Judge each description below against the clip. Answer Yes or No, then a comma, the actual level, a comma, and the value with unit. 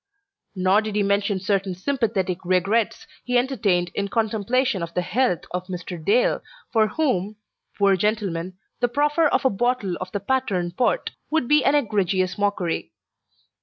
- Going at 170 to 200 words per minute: No, average, 155 wpm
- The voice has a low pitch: No, high, 205 Hz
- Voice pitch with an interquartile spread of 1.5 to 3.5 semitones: No, average, 4.9 semitones